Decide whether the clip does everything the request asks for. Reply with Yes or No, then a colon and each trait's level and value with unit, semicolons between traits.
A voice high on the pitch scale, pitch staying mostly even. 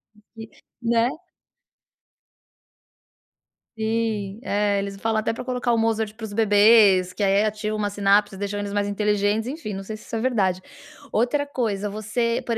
Yes: high, 215 Hz; narrow, 1.9 semitones